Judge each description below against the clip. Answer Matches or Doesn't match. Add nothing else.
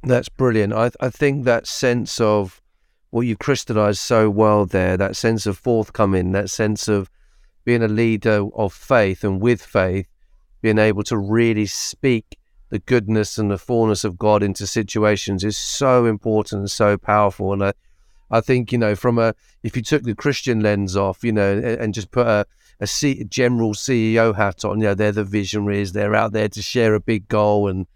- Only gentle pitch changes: Matches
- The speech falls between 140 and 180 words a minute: Doesn't match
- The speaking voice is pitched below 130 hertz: Matches